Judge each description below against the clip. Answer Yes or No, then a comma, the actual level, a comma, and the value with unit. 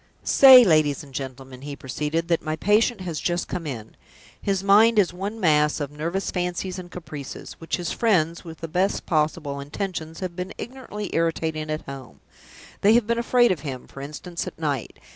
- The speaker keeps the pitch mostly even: No, average, 4.5 semitones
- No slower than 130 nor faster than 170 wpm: No, average, 185 wpm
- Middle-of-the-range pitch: Yes, medium, 165 Hz